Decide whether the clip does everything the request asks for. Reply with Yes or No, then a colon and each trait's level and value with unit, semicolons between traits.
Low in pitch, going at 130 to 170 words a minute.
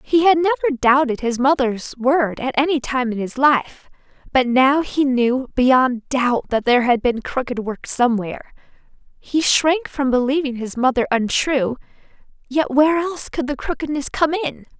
No: very high, 265 Hz; average, 165 wpm